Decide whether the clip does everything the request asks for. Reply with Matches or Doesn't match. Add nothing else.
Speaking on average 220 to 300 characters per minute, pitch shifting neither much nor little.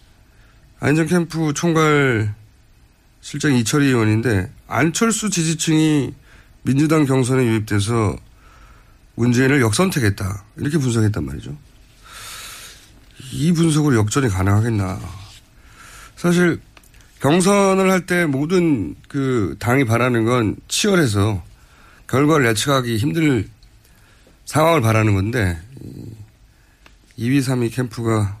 Doesn't match